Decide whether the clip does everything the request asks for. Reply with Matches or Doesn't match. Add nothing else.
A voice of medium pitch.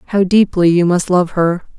Matches